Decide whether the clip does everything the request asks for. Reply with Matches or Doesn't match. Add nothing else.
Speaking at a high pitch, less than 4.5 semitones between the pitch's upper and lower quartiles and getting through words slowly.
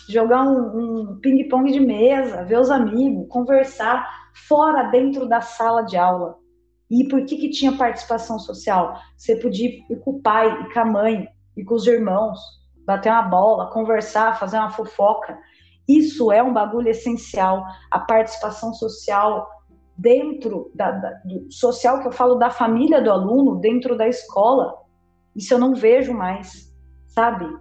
Doesn't match